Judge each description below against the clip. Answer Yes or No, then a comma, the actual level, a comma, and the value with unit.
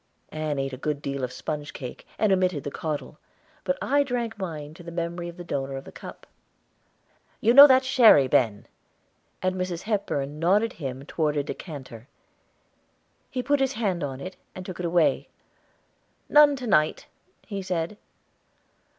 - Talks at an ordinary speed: Yes, average, 165 wpm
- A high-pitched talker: No, medium, 170 Hz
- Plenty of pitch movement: Yes, wide, 6.6 semitones